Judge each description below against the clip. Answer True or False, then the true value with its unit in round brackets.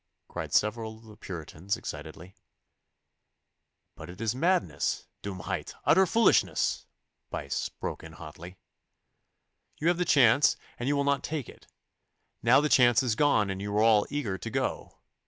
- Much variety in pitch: True (6.8 semitones)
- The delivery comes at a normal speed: True (155 wpm)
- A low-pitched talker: True (110 Hz)